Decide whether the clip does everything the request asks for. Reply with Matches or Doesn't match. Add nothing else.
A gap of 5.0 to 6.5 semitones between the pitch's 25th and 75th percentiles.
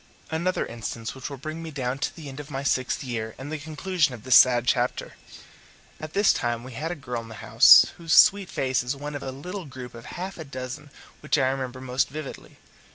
Doesn't match